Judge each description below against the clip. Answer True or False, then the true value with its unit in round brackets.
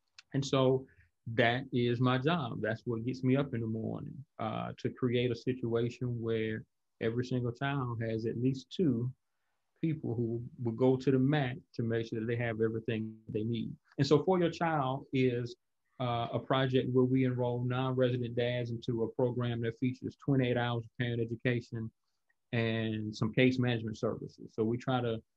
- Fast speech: False (180 wpm)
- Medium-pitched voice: False (120 Hz)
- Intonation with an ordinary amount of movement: False (2.1 semitones)